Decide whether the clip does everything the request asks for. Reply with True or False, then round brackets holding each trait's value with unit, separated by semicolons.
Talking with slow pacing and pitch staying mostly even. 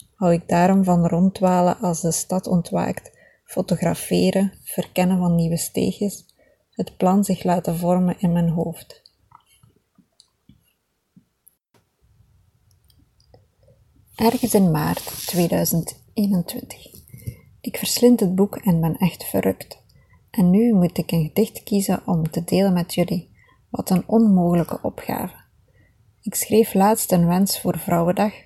False (120 wpm; 3.2 semitones)